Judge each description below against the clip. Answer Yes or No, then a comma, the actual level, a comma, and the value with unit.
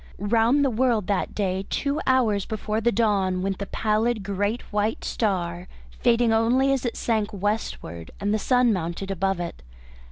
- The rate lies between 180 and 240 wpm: No, average, 165 wpm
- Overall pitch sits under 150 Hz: No, high, 210 Hz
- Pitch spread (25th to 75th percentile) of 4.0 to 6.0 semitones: No, average, 3.3 semitones